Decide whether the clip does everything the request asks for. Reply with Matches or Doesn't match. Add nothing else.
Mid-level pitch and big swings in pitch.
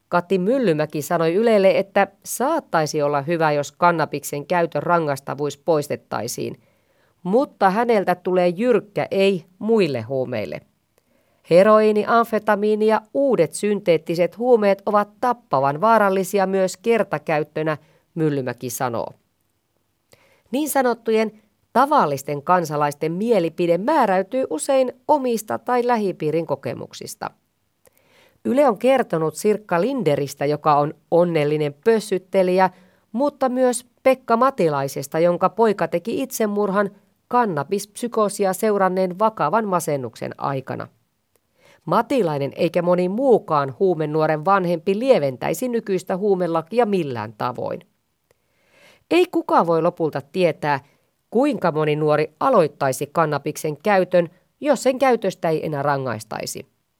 Matches